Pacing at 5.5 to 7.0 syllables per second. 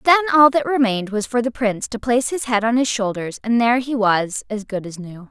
Yes: 5.9 syllables/s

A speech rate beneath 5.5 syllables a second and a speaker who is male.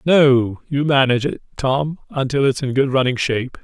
Yes: 5.1 syllables/s; male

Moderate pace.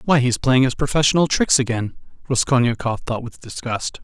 Yes: average, 165 wpm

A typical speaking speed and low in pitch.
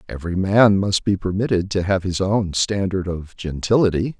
Yes: average, 170 wpm; very low, 95 Hz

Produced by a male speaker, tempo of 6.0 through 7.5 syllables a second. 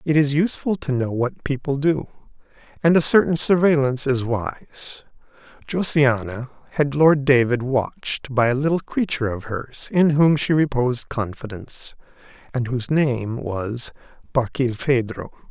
No: male; 4.8 syllables/s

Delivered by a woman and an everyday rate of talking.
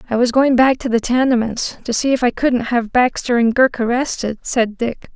No: female; fast, 220 wpm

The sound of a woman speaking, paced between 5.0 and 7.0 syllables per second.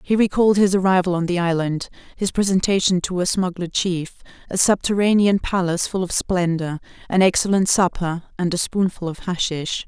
Yes: female; 5.4 syllables/s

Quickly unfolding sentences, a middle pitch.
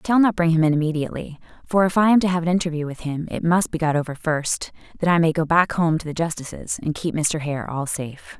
Yes: fast, 270 wpm; medium, 160 Hz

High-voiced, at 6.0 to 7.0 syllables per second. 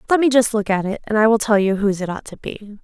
Yes: high, 215 Hz; 6.7 syllables/s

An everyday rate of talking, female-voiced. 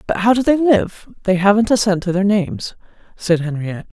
Yes: average, 195 wpm; female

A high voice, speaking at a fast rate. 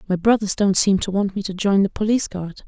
Yes: high, 195 Hz; fast, 270 wpm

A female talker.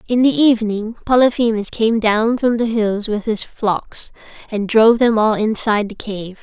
Yes: female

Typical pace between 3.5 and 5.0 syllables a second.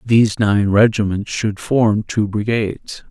Yes: 4.0 syllables/s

